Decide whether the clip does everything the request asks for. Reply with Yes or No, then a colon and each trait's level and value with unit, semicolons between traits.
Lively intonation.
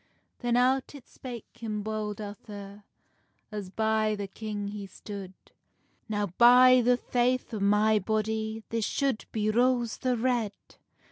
No: average, 2.7 semitones